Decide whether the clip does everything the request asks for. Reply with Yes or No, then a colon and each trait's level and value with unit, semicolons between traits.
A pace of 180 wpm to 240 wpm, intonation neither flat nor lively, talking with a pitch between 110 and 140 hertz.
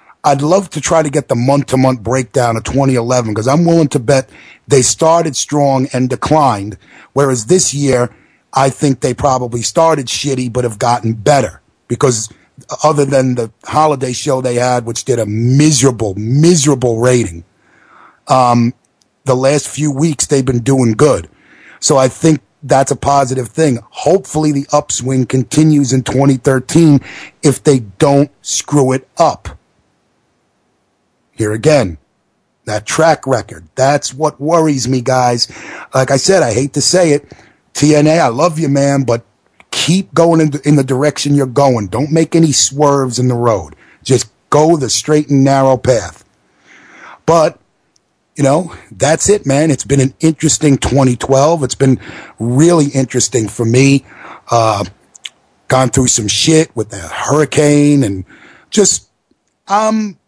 No: average, 150 wpm; average, 3.5 semitones; low, 135 Hz